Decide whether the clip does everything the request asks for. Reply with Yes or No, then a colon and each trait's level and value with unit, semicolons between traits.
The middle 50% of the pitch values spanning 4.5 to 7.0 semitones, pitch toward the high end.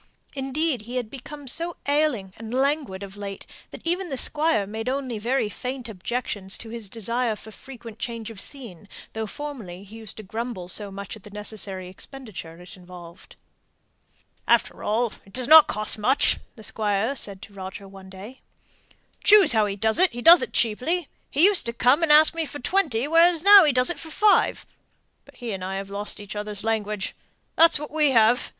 Yes: wide, 5.6 semitones; high, 230 Hz